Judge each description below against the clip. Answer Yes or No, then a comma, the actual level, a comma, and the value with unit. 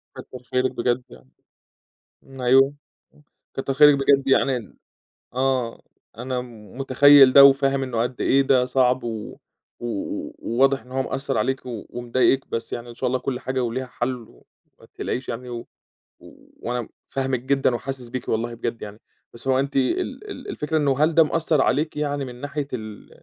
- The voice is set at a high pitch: No, low, 130 Hz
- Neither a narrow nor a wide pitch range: No, narrow, 2.1 semitones